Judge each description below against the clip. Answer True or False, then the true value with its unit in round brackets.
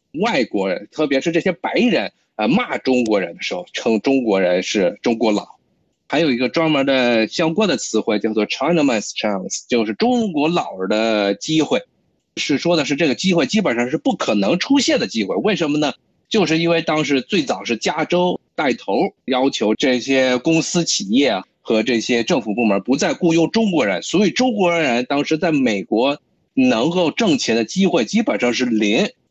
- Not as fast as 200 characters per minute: False (290 characters per minute)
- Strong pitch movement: True (6.7 semitones)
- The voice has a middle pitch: True (155 Hz)